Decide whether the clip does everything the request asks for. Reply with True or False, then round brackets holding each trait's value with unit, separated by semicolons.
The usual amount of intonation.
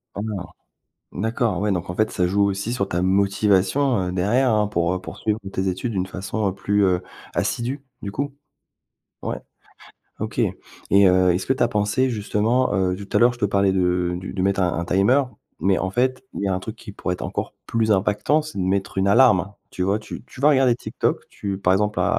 True (3.6 semitones)